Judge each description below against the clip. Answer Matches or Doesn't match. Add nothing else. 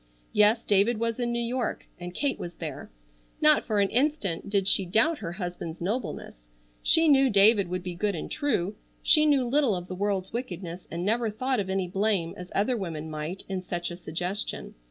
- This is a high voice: Matches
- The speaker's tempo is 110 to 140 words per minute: Doesn't match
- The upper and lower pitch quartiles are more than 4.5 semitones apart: Matches